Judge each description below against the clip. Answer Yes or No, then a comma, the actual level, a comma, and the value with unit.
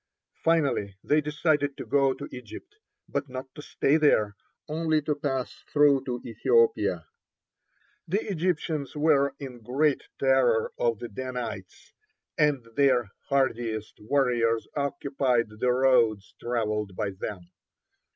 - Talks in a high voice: No, low, 135 Hz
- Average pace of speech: No, slow, 120 wpm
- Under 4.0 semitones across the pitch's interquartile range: No, average, 4.3 semitones